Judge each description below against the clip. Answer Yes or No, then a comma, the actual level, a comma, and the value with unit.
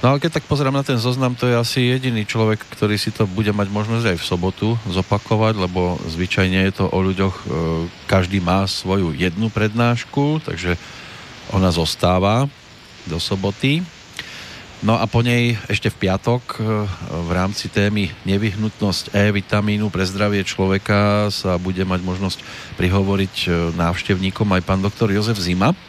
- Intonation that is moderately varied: Yes, average, 3.2 semitones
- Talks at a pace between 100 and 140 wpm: No, average, 150 wpm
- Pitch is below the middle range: Yes, low, 100 Hz